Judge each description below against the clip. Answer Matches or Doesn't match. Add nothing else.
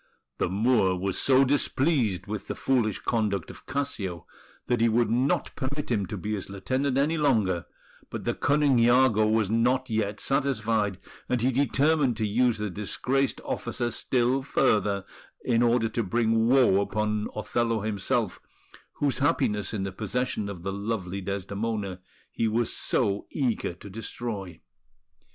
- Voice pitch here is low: Matches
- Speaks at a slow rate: Doesn't match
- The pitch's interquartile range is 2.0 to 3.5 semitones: Doesn't match